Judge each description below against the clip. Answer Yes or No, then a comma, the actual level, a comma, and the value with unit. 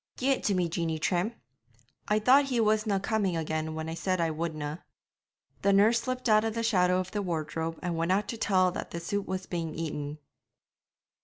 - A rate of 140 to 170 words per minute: No, fast, 205 wpm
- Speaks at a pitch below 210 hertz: Yes, medium, 185 Hz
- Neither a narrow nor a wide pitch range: Yes, average, 4.6 semitones